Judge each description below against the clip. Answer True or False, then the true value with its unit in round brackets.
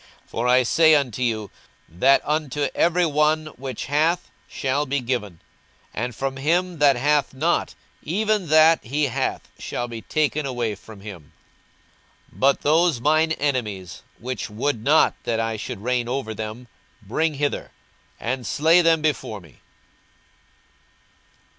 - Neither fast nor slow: True (145 wpm)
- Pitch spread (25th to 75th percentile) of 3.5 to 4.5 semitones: False (4.9 semitones)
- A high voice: False (135 Hz)